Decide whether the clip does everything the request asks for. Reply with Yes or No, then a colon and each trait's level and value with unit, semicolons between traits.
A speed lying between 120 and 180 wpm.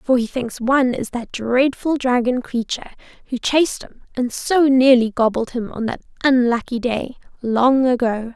Yes: average, 165 wpm